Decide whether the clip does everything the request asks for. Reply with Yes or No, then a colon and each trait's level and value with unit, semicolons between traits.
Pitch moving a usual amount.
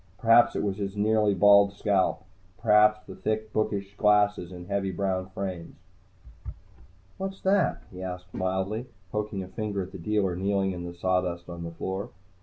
No: narrow, 2.3 semitones